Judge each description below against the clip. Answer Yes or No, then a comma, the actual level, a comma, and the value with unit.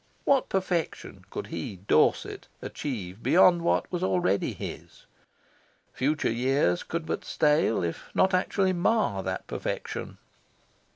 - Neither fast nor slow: No, slow, 120 wpm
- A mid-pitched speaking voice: Yes, medium, 155 Hz